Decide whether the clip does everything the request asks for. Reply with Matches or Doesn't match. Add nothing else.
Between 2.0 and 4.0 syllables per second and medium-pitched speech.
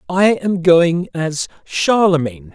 Matches